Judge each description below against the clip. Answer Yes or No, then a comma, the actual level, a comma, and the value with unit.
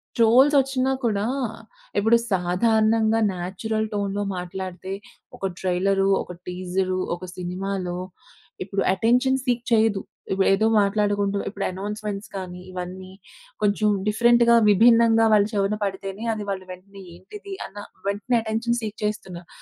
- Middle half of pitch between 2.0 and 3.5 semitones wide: Yes, average, 3.0 semitones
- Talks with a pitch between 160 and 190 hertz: No, high, 200 Hz